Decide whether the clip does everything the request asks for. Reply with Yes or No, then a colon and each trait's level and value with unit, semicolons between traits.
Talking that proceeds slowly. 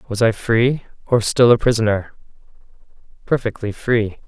Yes: slow, 125 wpm